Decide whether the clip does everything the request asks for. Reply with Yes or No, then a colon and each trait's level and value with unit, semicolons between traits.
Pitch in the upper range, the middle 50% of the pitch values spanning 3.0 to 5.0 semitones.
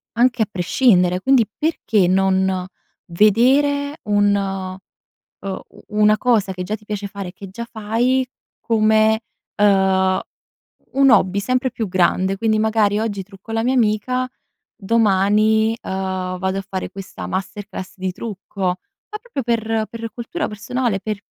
Yes: high, 210 Hz; average, 3.3 semitones